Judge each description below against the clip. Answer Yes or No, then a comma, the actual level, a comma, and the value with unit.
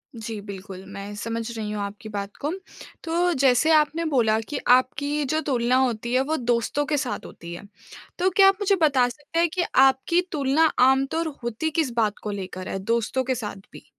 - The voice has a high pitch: Yes, very high, 255 Hz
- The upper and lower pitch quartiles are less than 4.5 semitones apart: No, wide, 5.6 semitones